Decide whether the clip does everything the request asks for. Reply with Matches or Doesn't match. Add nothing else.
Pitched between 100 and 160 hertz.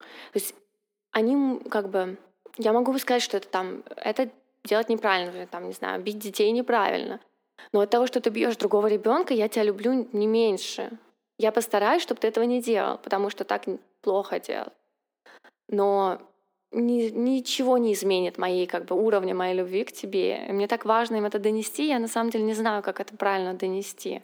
Doesn't match